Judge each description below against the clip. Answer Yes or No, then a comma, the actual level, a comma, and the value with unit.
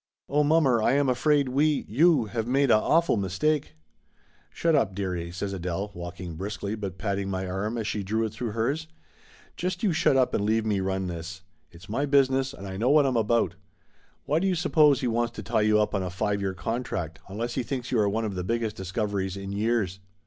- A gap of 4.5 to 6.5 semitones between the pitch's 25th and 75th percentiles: Yes, wide, 5.5 semitones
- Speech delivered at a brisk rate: Yes, fast, 220 wpm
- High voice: No, low, 110 Hz